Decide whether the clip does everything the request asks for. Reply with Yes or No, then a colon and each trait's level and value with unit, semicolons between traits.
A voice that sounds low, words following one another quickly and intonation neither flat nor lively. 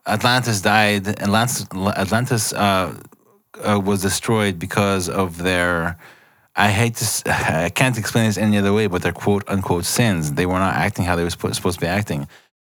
No: low, 100 Hz; average, 175 wpm; average, 3.0 semitones